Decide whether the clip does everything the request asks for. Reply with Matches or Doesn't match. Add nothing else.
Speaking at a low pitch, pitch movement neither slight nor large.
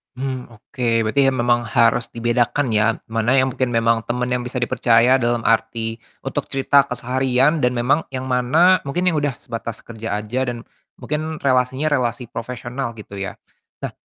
Doesn't match